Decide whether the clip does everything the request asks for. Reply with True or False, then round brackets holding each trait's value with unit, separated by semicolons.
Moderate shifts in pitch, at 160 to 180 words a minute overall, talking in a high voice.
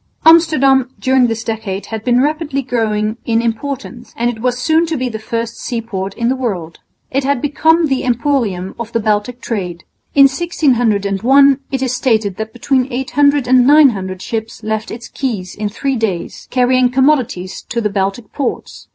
True (3.6 semitones; 170 wpm; 240 Hz)